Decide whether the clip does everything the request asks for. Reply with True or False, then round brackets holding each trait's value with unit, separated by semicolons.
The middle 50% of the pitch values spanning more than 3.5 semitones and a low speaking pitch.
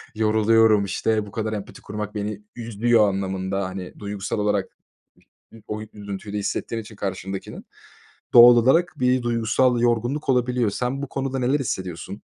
False (3.1 semitones; 110 Hz)